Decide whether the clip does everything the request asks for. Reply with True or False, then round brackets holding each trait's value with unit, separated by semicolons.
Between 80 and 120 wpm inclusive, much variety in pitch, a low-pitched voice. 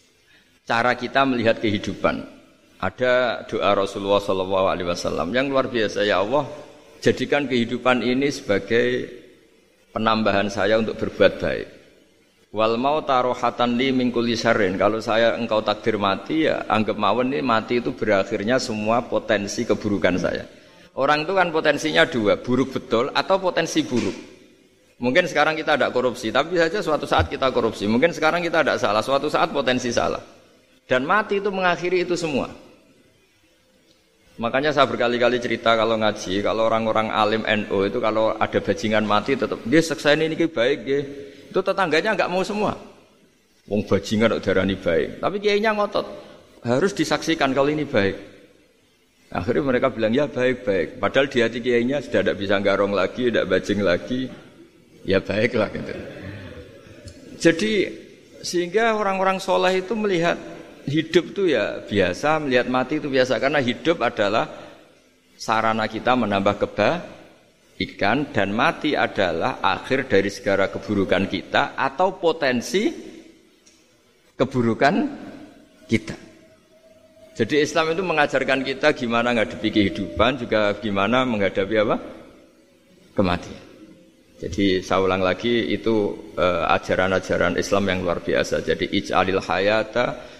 False (130 wpm; 6.6 semitones; 125 Hz)